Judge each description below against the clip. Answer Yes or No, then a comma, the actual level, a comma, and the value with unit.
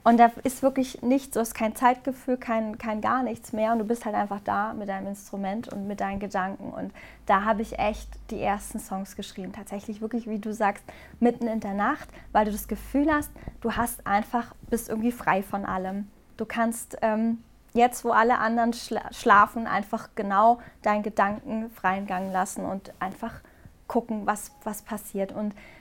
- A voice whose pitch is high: Yes, high, 220 Hz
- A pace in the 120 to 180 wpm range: No, fast, 190 wpm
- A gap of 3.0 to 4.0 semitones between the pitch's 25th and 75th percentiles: No, narrow, 2.5 semitones